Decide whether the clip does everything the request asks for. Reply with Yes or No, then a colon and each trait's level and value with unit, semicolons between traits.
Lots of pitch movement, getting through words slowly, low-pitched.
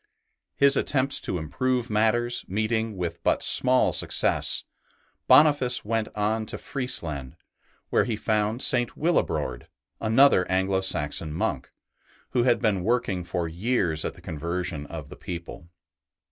Yes: wide, 5.7 semitones; slow, 130 wpm; low, 105 Hz